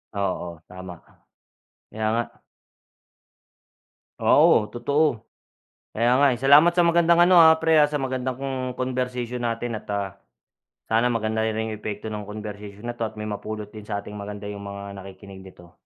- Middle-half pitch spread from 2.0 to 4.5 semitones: Yes, average, 4.0 semitones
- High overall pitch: No, low, 110 Hz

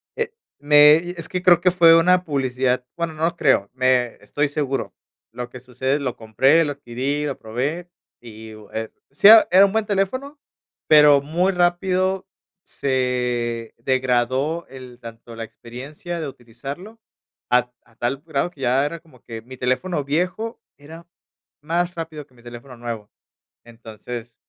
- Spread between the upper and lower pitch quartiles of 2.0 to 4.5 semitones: No, wide, 5.5 semitones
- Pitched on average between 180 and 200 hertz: No, medium, 140 Hz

